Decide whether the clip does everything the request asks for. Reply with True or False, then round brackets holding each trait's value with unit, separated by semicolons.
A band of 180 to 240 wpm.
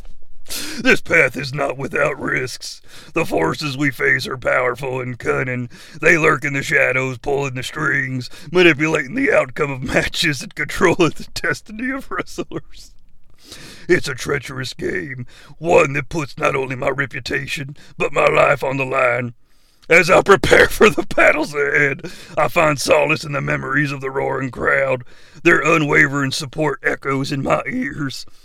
False (155 wpm)